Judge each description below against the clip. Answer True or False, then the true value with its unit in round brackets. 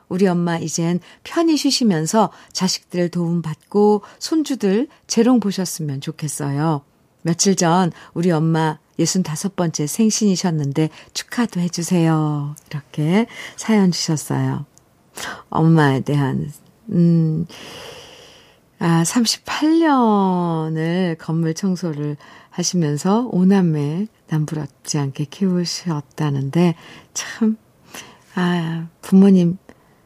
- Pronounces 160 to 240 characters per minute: True (200 characters per minute)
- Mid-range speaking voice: True (170 Hz)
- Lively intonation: False (4.0 semitones)